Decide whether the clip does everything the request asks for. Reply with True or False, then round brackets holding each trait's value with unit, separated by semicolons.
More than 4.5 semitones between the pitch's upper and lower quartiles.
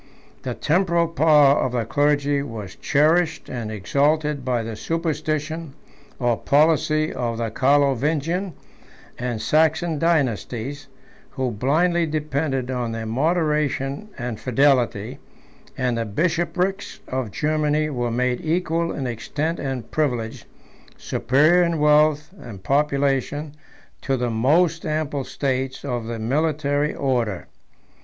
False (4.0 semitones)